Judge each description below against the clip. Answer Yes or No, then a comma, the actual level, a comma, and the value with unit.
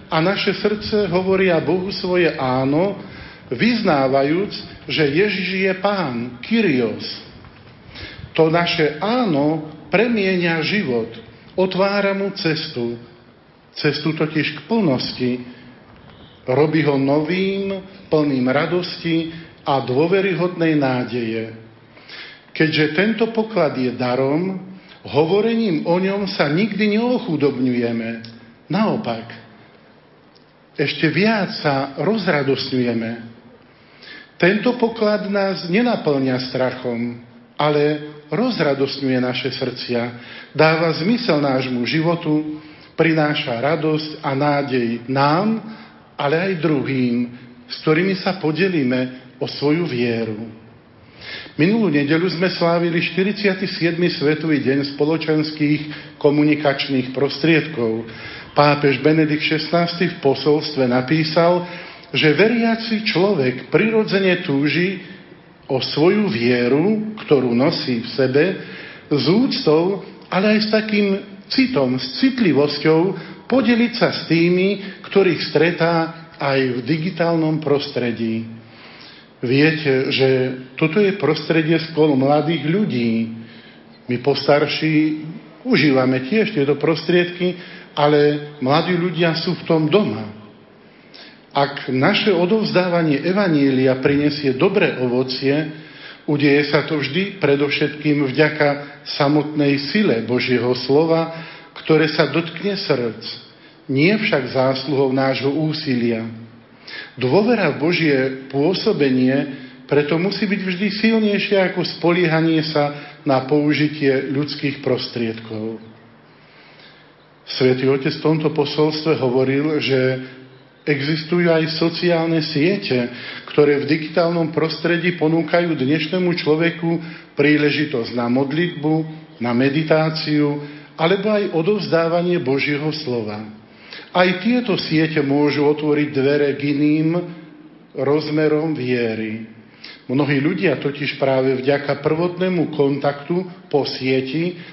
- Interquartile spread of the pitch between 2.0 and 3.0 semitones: No, average, 4.6 semitones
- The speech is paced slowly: Yes, slow, 95 wpm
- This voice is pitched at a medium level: Yes, medium, 150 Hz